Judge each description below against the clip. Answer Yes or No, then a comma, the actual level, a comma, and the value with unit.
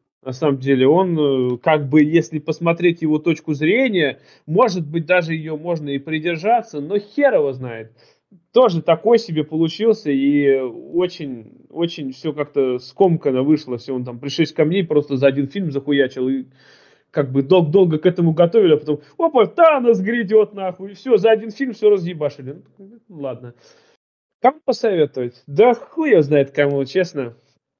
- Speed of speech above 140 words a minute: Yes, fast, 160 wpm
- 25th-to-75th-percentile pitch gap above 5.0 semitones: Yes, wide, 5.5 semitones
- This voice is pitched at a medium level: Yes, medium, 155 Hz